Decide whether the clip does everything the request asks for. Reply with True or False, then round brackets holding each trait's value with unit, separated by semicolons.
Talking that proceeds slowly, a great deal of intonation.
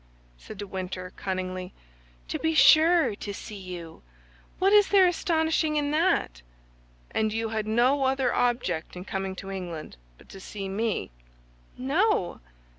False (145 wpm; 8.5 semitones)